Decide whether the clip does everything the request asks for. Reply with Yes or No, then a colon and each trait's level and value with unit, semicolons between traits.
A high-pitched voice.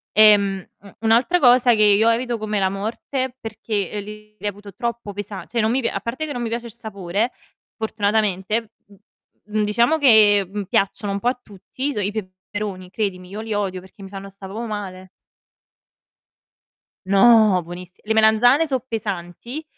Yes: high, 210 Hz